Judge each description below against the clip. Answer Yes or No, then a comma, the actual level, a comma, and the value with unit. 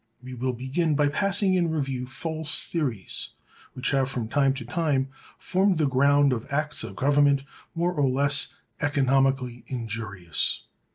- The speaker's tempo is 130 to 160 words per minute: Yes, average, 150 wpm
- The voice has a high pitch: No, low, 135 Hz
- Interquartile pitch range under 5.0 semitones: Yes, average, 3.0 semitones